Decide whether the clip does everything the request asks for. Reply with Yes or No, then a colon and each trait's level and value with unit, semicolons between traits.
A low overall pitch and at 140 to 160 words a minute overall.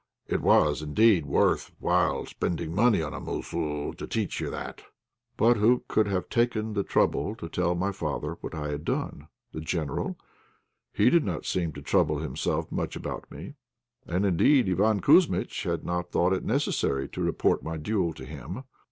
No: very low, 90 Hz; average, 180 wpm